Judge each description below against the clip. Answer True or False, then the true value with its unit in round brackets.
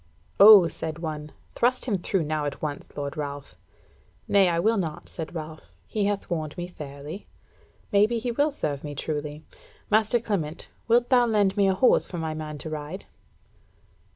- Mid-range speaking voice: True (170 Hz)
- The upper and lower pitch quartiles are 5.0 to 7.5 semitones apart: True (5.5 semitones)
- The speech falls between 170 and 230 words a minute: True (175 wpm)